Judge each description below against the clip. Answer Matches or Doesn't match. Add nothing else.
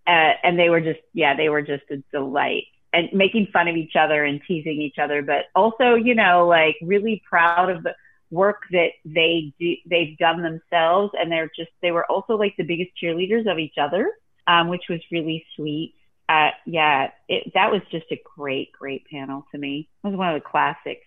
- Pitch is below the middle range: Doesn't match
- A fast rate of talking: Matches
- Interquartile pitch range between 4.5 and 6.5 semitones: Doesn't match